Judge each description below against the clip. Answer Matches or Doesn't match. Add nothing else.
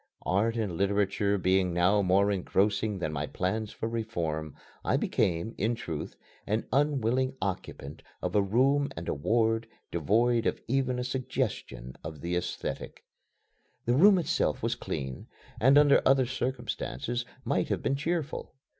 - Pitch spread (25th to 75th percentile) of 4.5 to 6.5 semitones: Matches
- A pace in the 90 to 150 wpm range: Matches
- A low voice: Matches